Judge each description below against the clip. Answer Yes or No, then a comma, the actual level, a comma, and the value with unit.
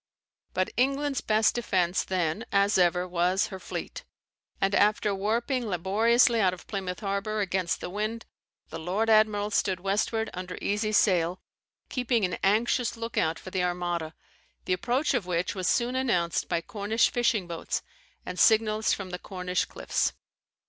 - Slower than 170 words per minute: Yes, average, 160 wpm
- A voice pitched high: Yes, high, 200 Hz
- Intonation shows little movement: No, average, 3.7 semitones